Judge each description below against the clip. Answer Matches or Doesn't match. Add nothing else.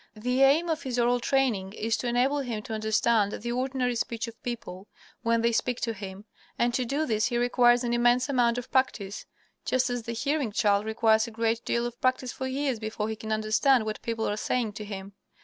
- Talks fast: Matches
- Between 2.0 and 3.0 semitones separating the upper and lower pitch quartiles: Matches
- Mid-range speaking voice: Doesn't match